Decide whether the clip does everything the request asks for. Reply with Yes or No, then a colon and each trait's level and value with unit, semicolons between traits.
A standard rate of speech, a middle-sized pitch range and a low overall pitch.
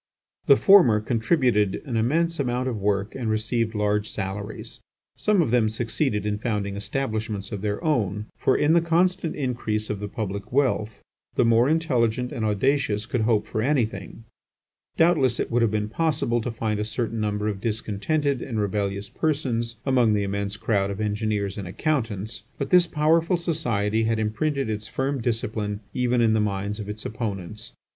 Yes: average, 170 wpm; average, 4.0 semitones; low, 110 Hz